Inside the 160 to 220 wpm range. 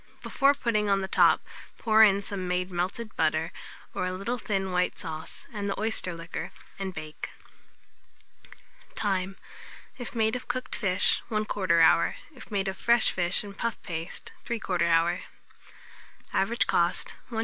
No: average, 150 wpm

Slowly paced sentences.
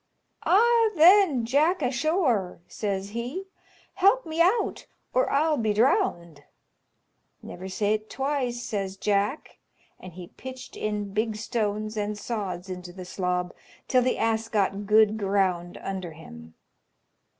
Yes: slow, 130 wpm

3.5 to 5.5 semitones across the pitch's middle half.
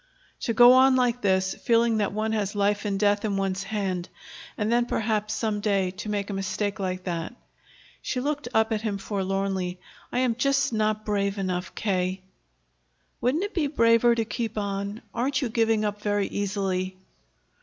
No: average, 2.8 semitones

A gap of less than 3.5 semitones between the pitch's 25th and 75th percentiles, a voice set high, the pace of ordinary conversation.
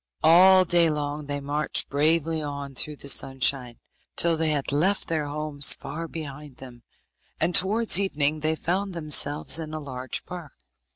No: average, 2.7 semitones; medium, 150 Hz; average, 160 wpm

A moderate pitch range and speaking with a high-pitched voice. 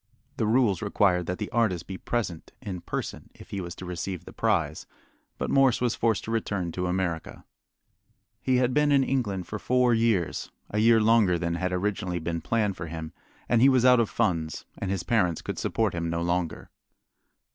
No: average, 4.8 semitones; low, 100 Hz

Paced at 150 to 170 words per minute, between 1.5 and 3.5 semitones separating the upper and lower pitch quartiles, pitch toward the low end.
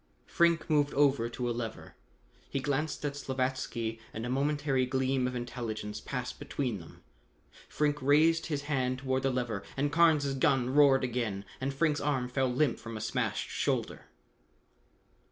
Yes: average, 155 wpm; average, 2.8 semitones; low, 130 Hz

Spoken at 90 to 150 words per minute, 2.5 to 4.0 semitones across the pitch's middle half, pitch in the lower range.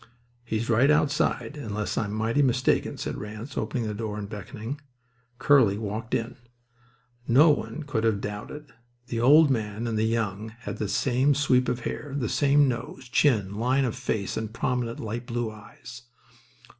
No: average, 165 wpm; average, 3.6 semitones; low, 115 Hz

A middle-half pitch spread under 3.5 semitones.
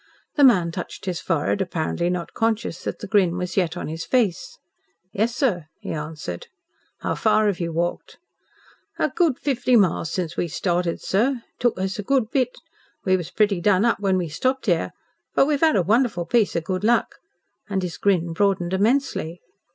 No: average, 5.1 semitones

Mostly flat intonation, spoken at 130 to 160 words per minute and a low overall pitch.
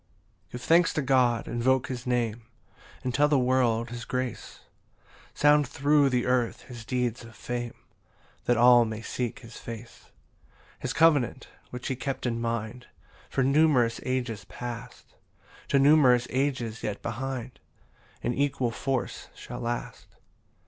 Yes: narrow, 2.1 semitones; average, 145 wpm; low, 125 Hz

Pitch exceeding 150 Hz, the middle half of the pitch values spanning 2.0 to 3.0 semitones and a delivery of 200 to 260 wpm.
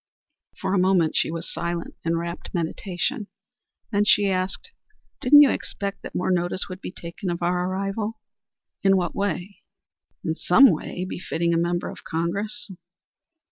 No: medium, 185 Hz; narrow, 2.6 semitones; average, 155 wpm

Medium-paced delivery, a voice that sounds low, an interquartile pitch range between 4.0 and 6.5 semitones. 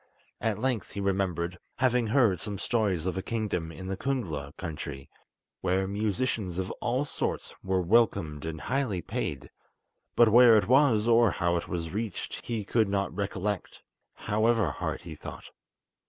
Yes: average, 155 wpm; low, 100 Hz; average, 4.6 semitones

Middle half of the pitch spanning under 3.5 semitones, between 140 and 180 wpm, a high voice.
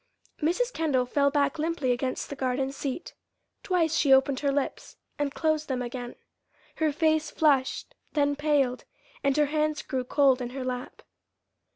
Yes: average, 2.9 semitones; average, 160 wpm; very high, 285 Hz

